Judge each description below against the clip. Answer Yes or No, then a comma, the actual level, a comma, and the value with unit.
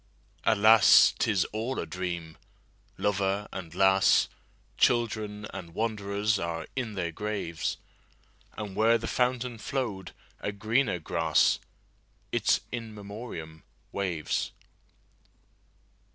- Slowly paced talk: Yes, slow, 90 wpm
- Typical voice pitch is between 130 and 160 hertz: No, low, 105 Hz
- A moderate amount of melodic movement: Yes, average, 3.3 semitones